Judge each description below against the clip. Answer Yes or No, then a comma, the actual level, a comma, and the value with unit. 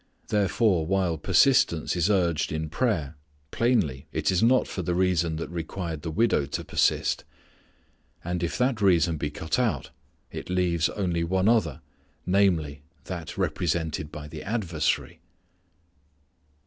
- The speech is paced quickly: No, slow, 135 wpm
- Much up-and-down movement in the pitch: No, average, 3.6 semitones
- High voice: No, very low, 85 Hz